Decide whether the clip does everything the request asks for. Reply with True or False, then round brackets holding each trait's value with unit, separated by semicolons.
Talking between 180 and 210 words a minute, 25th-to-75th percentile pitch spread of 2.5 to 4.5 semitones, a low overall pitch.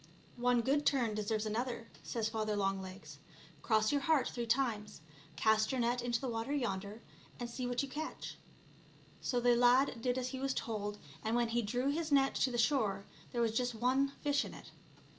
False (200 wpm; 3.2 semitones; 240 Hz)